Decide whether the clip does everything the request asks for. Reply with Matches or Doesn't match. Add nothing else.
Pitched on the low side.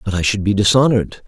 Matches